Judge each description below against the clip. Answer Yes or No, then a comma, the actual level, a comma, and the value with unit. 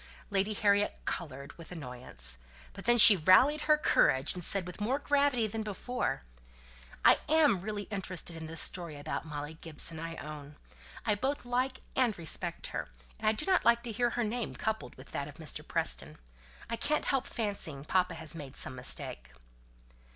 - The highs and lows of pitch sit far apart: Yes, wide, 7.4 semitones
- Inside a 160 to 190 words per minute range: Yes, average, 180 wpm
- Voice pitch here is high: Yes, high, 195 Hz